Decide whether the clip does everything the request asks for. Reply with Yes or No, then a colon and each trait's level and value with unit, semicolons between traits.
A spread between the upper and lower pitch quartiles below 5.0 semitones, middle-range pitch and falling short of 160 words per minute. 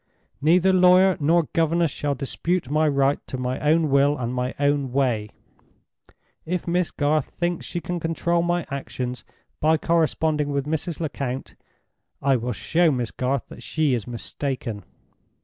Yes: average, 4.1 semitones; medium, 145 Hz; average, 150 wpm